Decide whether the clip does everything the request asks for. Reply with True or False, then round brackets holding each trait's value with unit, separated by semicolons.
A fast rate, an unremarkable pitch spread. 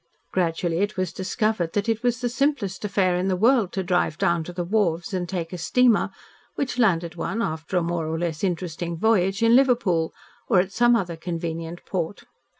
False (195 wpm; 4.3 semitones)